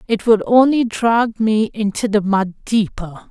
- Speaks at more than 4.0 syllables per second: No, 3.9 syllables/s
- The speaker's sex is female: Yes, female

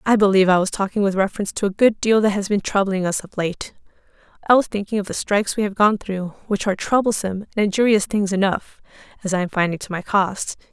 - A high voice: Yes, high, 200 Hz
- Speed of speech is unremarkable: No, fast, 235 wpm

